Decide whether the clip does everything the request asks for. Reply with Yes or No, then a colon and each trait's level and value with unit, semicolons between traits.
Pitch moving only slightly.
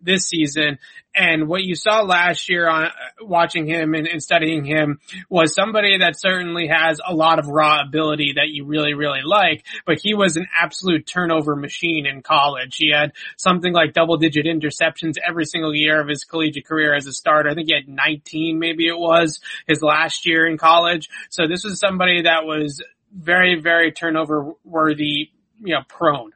Yes: narrow, 2.1 semitones